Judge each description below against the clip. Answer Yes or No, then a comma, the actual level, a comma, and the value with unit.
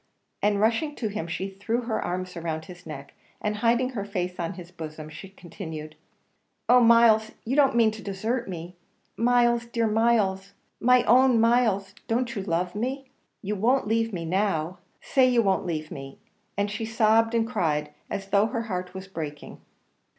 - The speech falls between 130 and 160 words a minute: No, average, 175 wpm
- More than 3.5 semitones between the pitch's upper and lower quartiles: Yes, average, 4.5 semitones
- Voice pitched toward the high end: Yes, high, 205 Hz